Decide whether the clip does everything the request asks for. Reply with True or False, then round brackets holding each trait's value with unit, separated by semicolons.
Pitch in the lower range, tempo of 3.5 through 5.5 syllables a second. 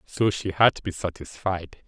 True (95 Hz; 4.6 syllables/s)